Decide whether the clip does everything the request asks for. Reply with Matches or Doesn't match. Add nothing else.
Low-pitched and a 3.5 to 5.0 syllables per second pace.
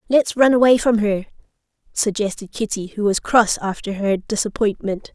Doesn't match